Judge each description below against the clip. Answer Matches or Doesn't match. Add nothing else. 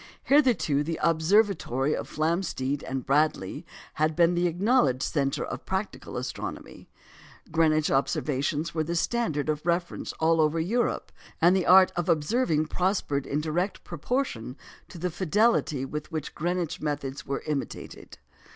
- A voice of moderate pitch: Matches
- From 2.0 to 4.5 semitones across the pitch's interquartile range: Matches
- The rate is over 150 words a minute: Doesn't match